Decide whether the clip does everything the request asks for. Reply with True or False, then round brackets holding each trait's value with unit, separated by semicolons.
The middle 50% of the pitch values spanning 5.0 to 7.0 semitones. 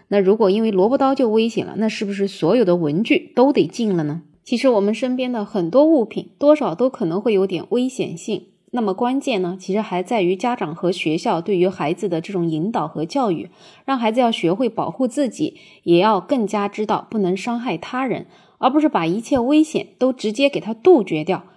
True (5.6 semitones)